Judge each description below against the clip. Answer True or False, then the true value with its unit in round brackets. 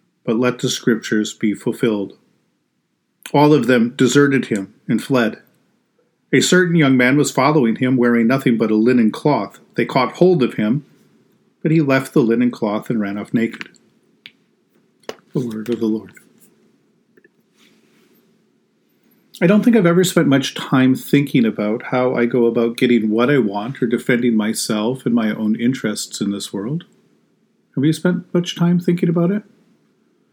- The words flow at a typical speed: True (160 wpm)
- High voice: False (125 Hz)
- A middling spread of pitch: False (5.9 semitones)